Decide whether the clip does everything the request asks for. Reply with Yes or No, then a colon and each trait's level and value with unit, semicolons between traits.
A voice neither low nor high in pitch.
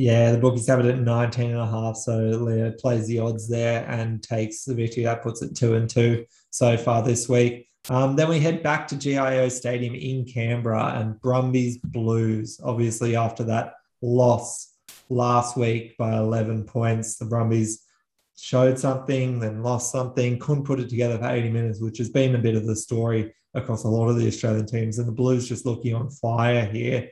No: low, 120 Hz